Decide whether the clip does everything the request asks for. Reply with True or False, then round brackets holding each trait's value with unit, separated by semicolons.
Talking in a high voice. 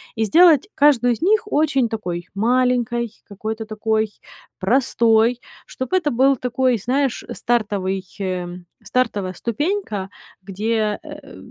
True (235 Hz)